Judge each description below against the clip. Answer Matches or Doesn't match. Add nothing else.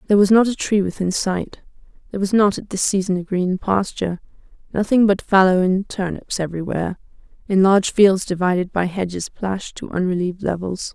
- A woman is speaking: Matches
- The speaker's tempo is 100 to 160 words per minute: Doesn't match